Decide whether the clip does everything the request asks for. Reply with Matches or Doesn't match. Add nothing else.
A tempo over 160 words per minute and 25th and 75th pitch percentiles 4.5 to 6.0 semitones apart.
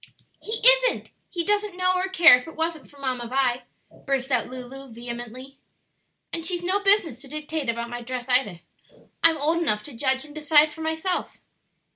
Matches